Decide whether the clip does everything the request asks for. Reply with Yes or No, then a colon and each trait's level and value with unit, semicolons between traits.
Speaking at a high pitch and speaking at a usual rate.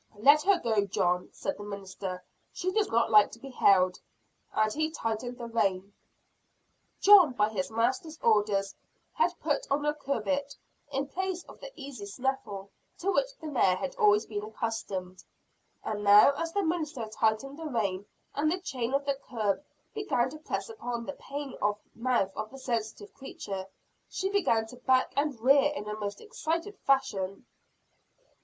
Yes: high, 245 Hz; average, 170 wpm